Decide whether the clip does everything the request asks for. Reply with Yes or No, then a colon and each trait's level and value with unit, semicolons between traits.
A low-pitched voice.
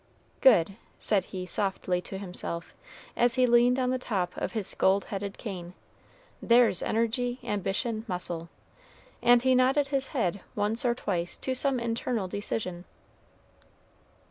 No: high, 220 Hz